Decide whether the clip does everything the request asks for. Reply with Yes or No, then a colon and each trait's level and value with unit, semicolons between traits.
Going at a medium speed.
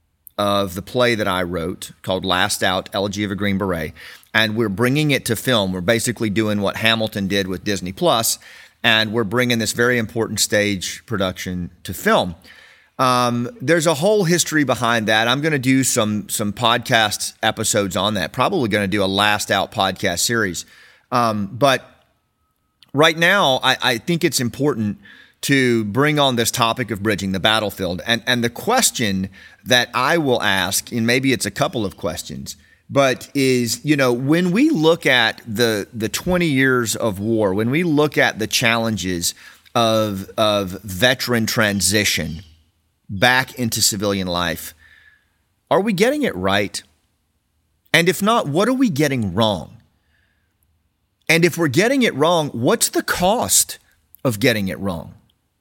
Yes: average, 165 wpm